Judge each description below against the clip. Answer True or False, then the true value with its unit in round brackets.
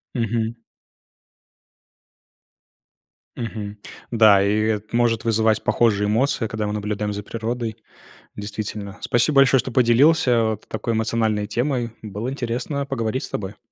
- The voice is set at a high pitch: False (110 Hz)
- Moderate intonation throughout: False (2.2 semitones)